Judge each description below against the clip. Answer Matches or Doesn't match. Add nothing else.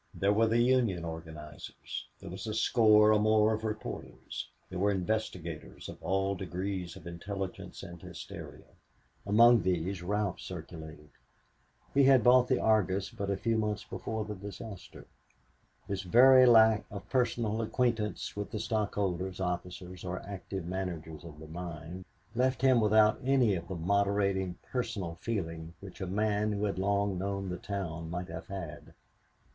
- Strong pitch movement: Doesn't match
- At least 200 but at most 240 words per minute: Doesn't match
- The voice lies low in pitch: Matches